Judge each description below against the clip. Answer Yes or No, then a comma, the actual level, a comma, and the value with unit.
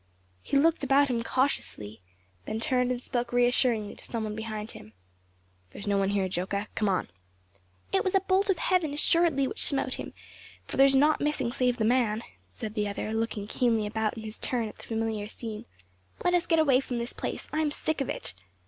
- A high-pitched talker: Yes, high, 240 Hz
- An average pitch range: Yes, average, 4.5 semitones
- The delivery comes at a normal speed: No, fast, 210 wpm